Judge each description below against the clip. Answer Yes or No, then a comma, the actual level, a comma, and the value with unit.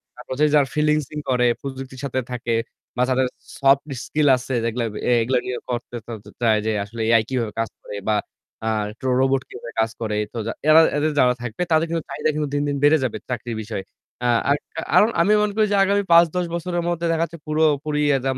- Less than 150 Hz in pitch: Yes, low, 135 Hz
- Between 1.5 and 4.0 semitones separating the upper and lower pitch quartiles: No, average, 4.4 semitones